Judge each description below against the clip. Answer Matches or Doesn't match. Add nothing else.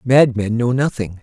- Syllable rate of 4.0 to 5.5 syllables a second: Matches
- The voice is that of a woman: Doesn't match